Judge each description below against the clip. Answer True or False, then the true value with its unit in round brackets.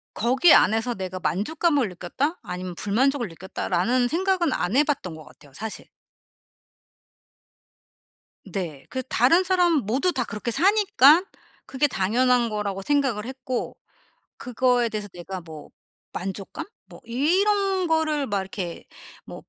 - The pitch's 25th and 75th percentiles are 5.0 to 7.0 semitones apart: False (7.5 semitones)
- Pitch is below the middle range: False (245 Hz)